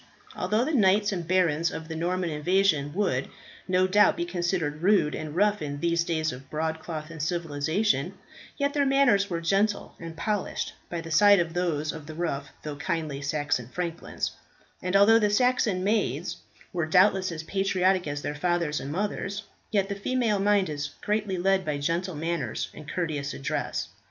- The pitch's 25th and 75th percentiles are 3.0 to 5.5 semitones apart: Yes, average, 4.2 semitones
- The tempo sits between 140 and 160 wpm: No, average, 175 wpm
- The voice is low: No, medium, 175 Hz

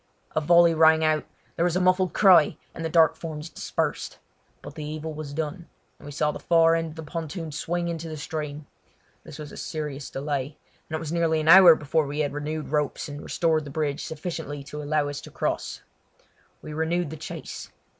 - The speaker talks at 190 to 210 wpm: Yes, fast, 205 wpm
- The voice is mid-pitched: Yes, medium, 155 Hz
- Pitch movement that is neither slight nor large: No, narrow, 1.8 semitones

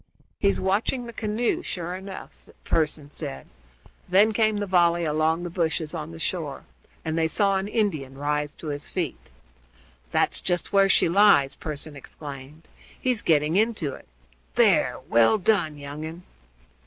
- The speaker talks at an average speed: Yes, average, 155 wpm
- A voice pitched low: No, medium, 165 Hz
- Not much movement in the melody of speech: No, average, 5.0 semitones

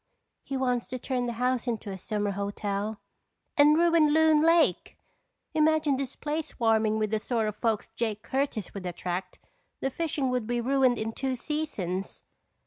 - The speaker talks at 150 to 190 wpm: Yes, average, 165 wpm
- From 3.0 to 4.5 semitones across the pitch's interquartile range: No, average, 5.2 semitones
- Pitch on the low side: No, high, 245 Hz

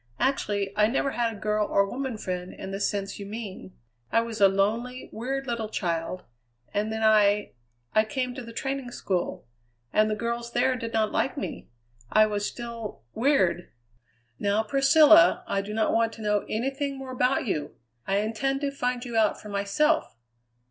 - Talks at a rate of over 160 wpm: Yes, average, 185 wpm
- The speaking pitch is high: Yes, high, 220 Hz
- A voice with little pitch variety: No, average, 3.8 semitones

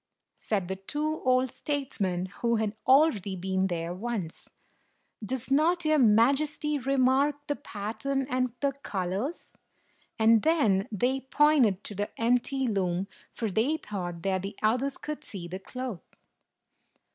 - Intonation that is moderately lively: No, wide, 6.1 semitones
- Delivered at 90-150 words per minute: Yes, slow, 135 wpm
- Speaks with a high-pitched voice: Yes, high, 235 Hz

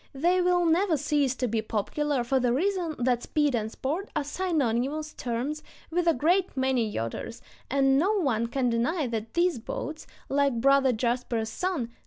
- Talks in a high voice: Yes, very high, 275 Hz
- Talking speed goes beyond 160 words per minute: Yes, average, 180 wpm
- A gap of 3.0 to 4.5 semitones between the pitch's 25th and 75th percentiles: No, average, 5.2 semitones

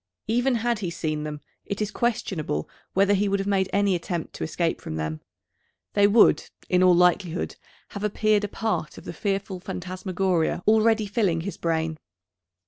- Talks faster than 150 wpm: Yes, average, 170 wpm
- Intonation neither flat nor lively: Yes, average, 3.6 semitones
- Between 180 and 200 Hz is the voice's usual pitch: Yes, high, 190 Hz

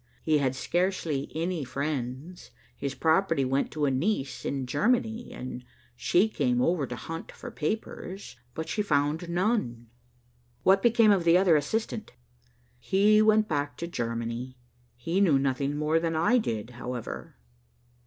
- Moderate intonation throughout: No, wide, 6.4 semitones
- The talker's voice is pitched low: No, medium, 155 Hz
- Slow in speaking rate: No, average, 145 wpm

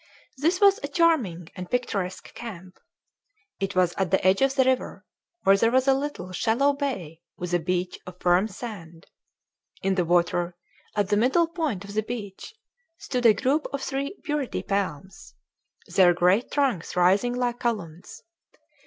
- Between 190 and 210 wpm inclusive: No, average, 160 wpm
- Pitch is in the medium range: No, high, 205 Hz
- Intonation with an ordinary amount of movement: No, wide, 6.8 semitones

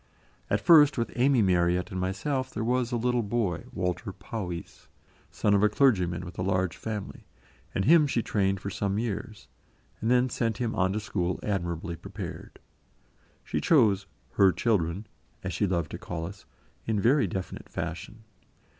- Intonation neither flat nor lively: Yes, average, 4.4 semitones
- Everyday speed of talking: Yes, average, 165 wpm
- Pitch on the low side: Yes, low, 100 Hz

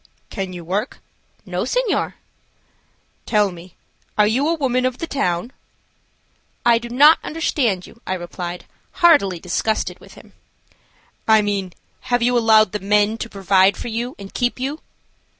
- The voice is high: Yes, high, 220 Hz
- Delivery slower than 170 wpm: Yes, average, 150 wpm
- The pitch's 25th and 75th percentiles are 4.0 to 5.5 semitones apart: Yes, average, 4.7 semitones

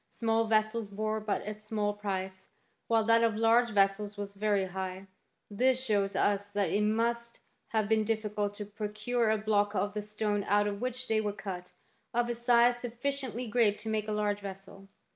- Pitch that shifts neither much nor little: No, narrow, 2.0 semitones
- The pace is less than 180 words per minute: No, average, 185 wpm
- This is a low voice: No, high, 210 Hz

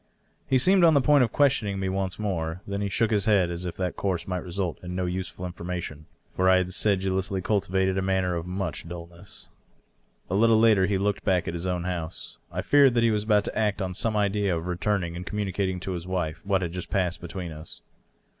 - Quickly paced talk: Yes, fast, 225 wpm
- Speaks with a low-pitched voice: Yes, very low, 95 Hz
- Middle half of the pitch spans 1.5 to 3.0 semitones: Yes, narrow, 2.5 semitones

